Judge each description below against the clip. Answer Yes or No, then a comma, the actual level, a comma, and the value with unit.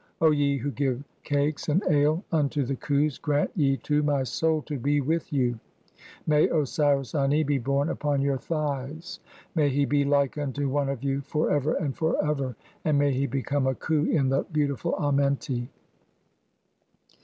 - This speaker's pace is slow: No, average, 175 wpm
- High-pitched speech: No, medium, 145 Hz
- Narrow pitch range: Yes, narrow, 1.6 semitones